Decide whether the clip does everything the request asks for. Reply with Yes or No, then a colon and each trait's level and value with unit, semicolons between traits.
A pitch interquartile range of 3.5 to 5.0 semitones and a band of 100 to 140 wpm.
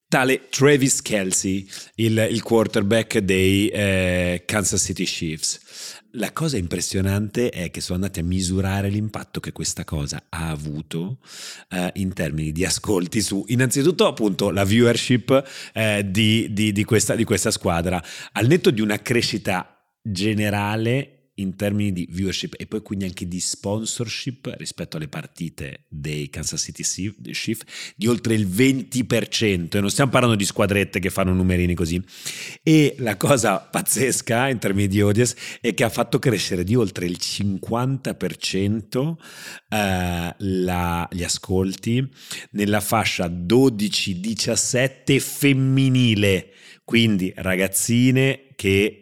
Yes: average, 4.2 semitones; average, 135 wpm